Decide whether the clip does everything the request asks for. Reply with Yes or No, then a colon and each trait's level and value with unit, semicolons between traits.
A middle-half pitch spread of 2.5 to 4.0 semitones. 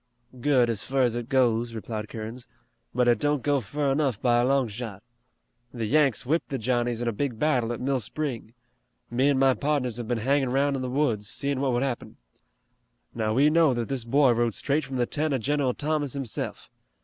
Yes: average, 3.0 semitones